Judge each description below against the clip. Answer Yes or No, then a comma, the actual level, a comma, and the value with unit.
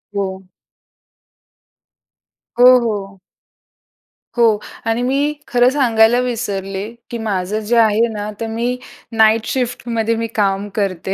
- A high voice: Yes, high, 225 Hz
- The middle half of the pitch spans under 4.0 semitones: Yes, average, 3.1 semitones